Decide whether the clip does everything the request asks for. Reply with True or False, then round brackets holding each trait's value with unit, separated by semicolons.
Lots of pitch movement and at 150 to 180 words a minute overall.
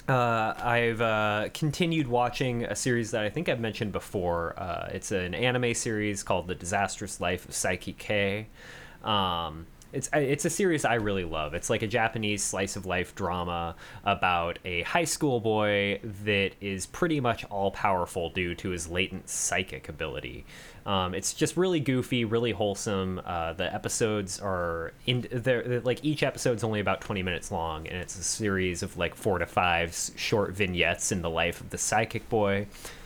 False (4.5 semitones; 175 wpm)